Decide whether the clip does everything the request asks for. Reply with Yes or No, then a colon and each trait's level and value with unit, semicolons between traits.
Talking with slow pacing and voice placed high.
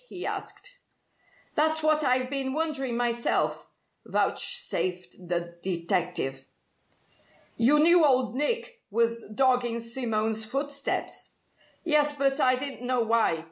Yes: slow, 110 wpm; very high, 255 Hz